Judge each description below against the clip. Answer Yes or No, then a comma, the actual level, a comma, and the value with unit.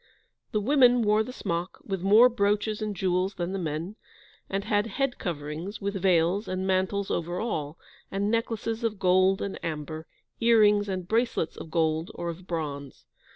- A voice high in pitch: Yes, high, 195 Hz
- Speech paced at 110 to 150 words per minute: No, average, 165 wpm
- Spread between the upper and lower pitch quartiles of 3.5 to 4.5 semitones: Yes, average, 3.9 semitones